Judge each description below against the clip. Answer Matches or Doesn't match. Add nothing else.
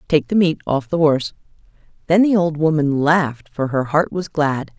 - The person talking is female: Matches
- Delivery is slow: Doesn't match